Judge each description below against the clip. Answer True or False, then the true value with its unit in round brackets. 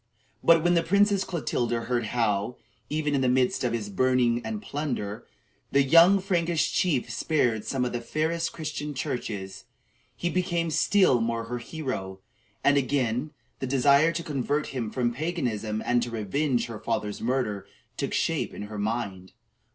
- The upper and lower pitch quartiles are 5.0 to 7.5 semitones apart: True (5.4 semitones)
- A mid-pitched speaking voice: False (130 Hz)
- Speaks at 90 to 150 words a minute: False (160 wpm)